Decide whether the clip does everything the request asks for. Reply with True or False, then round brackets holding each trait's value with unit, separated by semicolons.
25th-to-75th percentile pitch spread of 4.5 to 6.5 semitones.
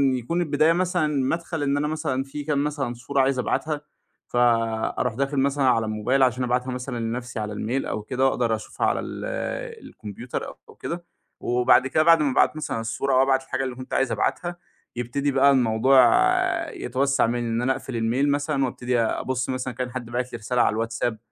False (2.8 semitones)